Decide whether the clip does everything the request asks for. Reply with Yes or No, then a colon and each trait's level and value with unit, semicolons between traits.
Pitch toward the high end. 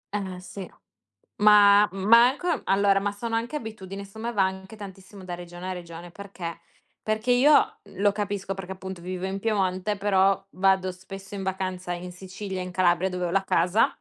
Yes: high, 195 Hz